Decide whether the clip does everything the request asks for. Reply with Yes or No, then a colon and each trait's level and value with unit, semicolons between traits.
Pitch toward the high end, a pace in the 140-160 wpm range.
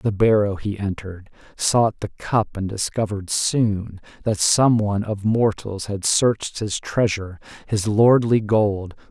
No: low, 105 Hz; average, 145 wpm